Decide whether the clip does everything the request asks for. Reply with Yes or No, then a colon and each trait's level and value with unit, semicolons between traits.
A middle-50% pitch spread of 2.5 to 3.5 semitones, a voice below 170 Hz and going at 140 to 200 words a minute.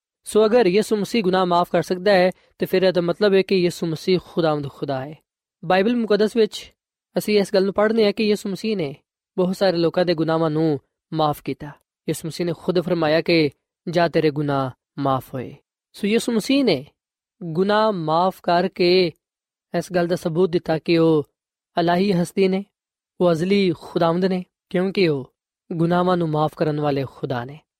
No: average, 3.0 semitones; medium, 175 Hz; fast, 165 wpm